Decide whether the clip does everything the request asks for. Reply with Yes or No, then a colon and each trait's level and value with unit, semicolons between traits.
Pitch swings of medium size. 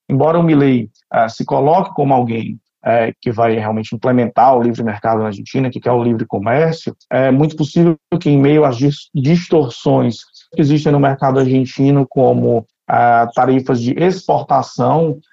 Yes: average, 4.2 semitones